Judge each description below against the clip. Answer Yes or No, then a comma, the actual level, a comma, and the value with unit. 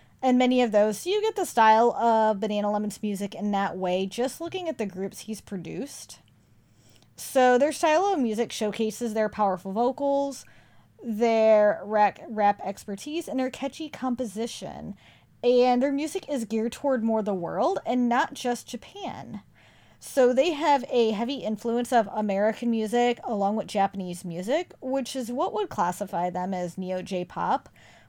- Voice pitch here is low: No, high, 225 Hz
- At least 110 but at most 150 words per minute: No, average, 160 wpm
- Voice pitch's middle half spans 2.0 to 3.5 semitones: No, average, 4.2 semitones